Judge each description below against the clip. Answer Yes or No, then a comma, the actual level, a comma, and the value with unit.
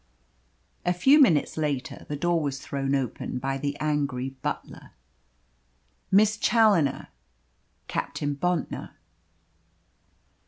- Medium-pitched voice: Yes, medium, 145 Hz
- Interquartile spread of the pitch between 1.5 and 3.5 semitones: No, average, 4.4 semitones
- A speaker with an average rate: No, slow, 95 wpm